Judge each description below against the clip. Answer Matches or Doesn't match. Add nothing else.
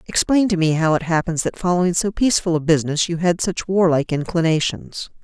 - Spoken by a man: Doesn't match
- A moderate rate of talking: Matches